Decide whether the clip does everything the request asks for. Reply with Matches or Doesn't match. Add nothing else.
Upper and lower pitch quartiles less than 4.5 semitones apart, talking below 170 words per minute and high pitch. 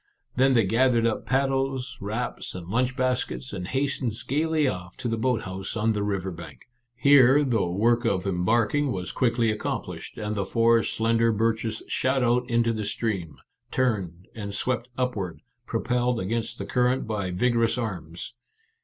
Doesn't match